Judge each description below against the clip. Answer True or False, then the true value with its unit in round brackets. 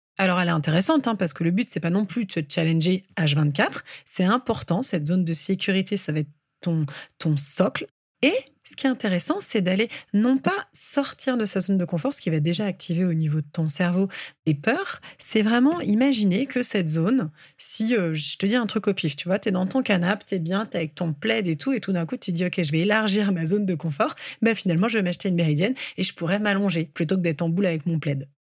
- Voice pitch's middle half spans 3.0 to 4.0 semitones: False (4.6 semitones)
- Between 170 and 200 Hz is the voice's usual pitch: True (185 Hz)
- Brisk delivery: True (255 wpm)